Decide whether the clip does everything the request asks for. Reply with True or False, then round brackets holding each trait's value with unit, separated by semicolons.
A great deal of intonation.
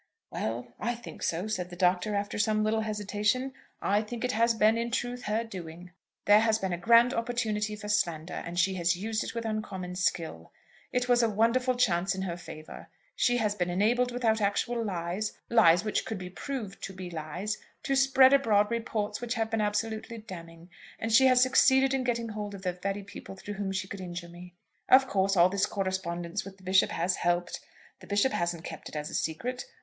False (4.3 semitones)